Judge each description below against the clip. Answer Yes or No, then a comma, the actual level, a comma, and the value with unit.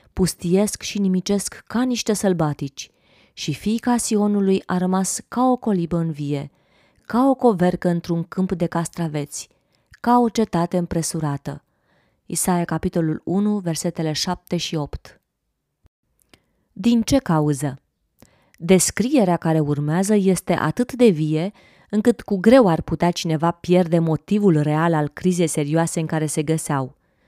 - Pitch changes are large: No, average, 4.4 semitones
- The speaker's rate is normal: Yes, average, 130 wpm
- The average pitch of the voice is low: No, medium, 175 Hz